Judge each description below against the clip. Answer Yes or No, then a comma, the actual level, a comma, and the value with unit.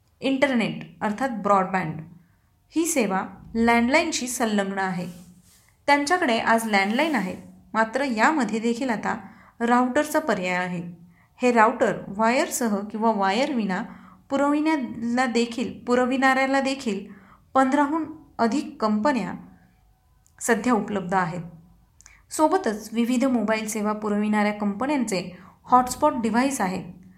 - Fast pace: No, average, 95 wpm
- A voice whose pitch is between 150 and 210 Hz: No, high, 230 Hz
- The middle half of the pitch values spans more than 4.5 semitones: Yes, average, 5.1 semitones